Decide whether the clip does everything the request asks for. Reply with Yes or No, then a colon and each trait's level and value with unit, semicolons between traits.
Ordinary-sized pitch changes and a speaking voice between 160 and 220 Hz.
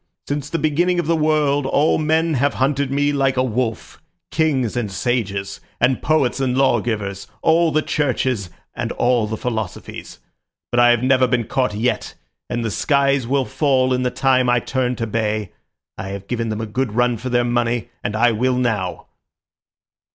No: average, 3.5 semitones; low, 125 Hz